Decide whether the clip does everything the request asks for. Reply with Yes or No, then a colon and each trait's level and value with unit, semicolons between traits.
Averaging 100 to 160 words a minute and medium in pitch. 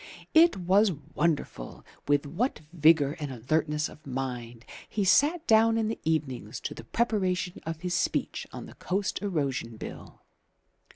Yes: average, 150 wpm; medium, 160 Hz